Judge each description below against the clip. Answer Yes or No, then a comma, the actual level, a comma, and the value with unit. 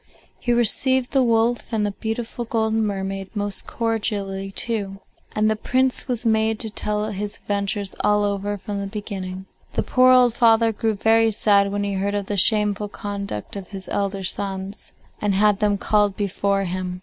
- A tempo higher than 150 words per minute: Yes, average, 175 wpm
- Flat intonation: Yes, narrow, 2.0 semitones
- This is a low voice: No, high, 205 Hz